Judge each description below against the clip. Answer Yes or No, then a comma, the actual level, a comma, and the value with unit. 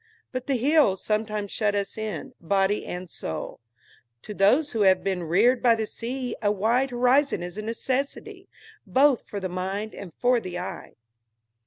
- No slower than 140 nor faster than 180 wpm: Yes, average, 170 wpm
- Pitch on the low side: No, high, 215 Hz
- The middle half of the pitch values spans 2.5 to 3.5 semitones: No, average, 4.6 semitones